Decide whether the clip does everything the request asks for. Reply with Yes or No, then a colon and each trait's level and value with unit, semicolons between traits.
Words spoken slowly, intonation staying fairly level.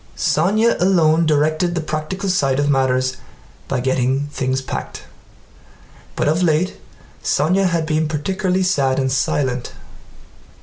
No: slow, 125 wpm; average, 4.9 semitones